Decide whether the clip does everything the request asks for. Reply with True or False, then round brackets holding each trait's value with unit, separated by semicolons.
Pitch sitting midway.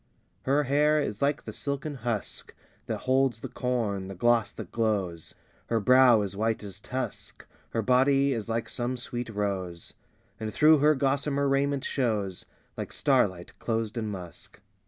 False (120 Hz)